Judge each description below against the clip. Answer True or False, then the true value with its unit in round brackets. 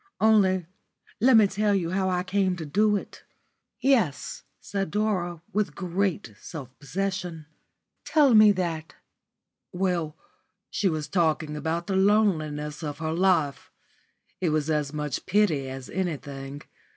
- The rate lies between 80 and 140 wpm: True (135 wpm)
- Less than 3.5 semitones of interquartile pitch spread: False (4.5 semitones)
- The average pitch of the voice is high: False (175 Hz)